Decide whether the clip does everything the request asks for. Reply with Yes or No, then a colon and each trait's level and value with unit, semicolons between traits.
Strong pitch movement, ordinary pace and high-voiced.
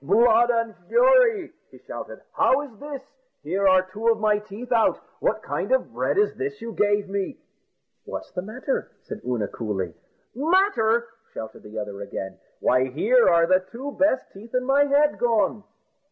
Yes: wide, 6.9 semitones; average, 170 wpm; high, 225 Hz